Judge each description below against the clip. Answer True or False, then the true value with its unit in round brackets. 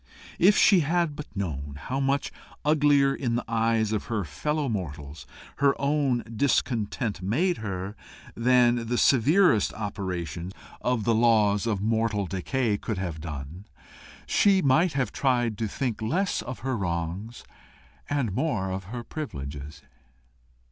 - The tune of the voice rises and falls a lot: True (6.1 semitones)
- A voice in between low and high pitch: False (115 Hz)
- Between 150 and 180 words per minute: False (140 wpm)